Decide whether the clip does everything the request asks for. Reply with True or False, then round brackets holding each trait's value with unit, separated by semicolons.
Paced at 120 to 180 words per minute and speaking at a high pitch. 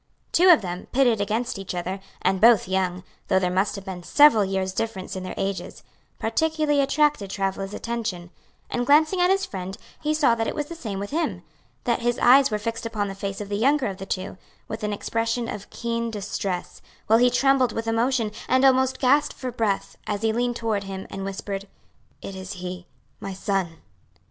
False (200 wpm; 220 Hz)